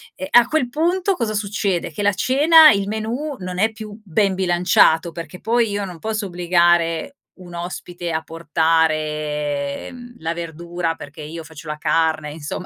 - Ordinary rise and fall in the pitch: Yes, average, 5.0 semitones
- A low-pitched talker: No, medium, 175 Hz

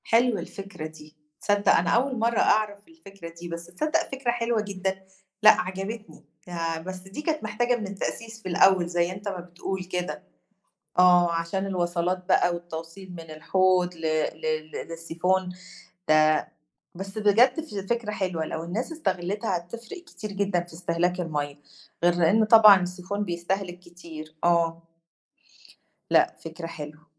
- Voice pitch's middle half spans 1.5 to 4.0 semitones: Yes, average, 3.5 semitones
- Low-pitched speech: No, medium, 185 Hz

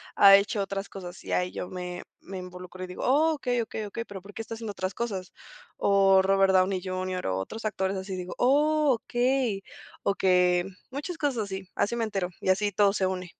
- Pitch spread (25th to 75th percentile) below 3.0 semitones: No, average, 3.3 semitones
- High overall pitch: Yes, high, 195 Hz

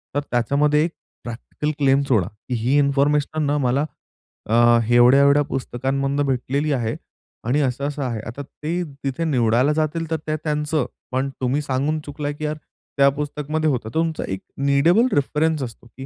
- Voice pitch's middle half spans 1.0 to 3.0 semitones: Yes, average, 2.7 semitones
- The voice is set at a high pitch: No, medium, 140 Hz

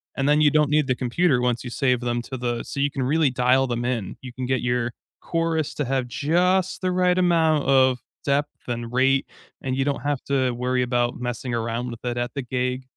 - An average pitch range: Yes, average, 3.0 semitones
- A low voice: Yes, low, 130 Hz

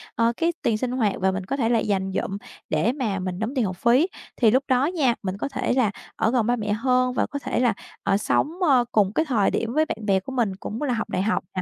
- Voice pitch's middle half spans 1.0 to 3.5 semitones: No, average, 4.2 semitones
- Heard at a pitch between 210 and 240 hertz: Yes, high, 230 Hz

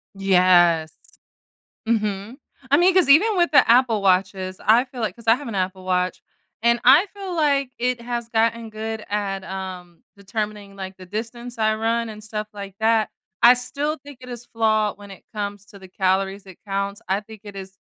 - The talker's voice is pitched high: Yes, high, 215 Hz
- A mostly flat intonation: No, average, 3.6 semitones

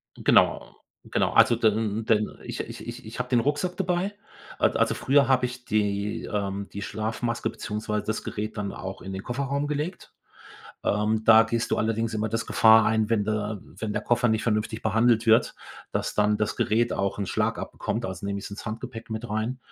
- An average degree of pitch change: No, narrow, 2.1 semitones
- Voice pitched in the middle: No, low, 110 Hz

